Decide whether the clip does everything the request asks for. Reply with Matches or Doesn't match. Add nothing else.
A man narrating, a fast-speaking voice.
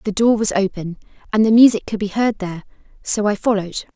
Doesn't match